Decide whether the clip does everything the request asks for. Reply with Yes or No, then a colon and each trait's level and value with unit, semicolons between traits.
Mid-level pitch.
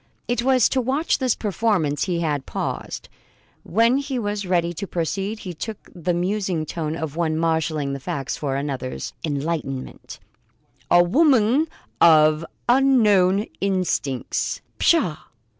Yes: medium, 180 Hz